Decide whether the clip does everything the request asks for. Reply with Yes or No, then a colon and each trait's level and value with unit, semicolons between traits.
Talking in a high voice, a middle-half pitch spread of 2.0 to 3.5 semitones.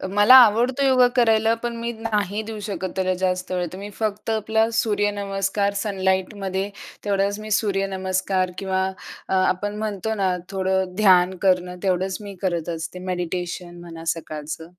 Yes: high, 195 Hz; narrow, 2.4 semitones